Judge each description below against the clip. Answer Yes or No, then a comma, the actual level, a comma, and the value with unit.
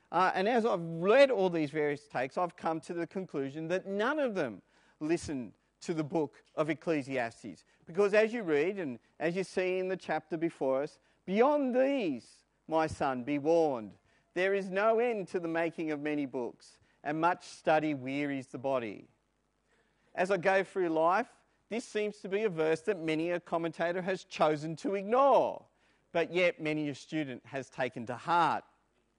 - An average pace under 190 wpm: Yes, average, 180 wpm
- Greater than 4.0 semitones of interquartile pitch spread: Yes, average, 4.4 semitones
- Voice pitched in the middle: Yes, medium, 165 Hz